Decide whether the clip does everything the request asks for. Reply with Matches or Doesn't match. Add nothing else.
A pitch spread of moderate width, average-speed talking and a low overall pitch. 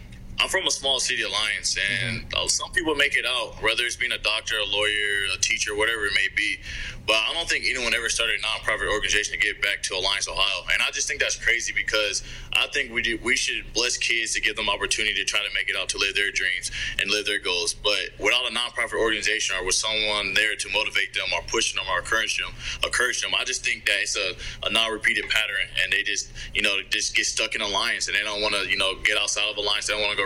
Doesn't match